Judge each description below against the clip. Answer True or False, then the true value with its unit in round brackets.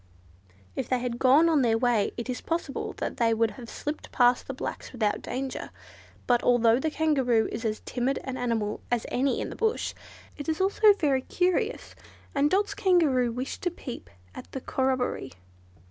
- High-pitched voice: True (260 Hz)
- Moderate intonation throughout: True (4.6 semitones)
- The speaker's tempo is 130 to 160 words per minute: False (180 wpm)